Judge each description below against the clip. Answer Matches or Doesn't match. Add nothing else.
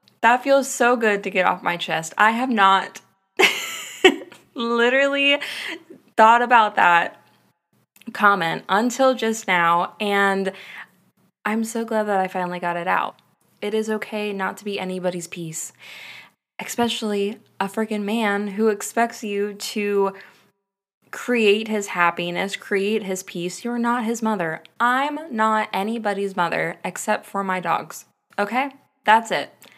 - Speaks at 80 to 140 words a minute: Matches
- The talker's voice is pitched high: Matches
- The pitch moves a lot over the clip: Doesn't match